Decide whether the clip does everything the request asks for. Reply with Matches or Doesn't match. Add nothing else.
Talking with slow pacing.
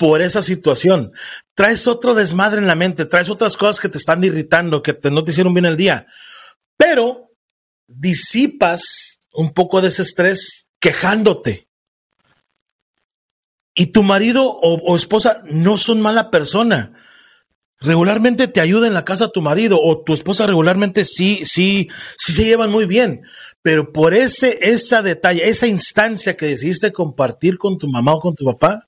Doesn't match